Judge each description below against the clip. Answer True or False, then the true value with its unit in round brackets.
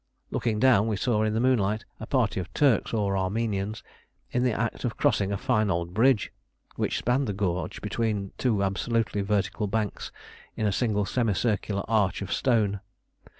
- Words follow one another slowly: False (170 wpm)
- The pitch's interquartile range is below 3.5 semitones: True (2.8 semitones)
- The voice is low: True (105 Hz)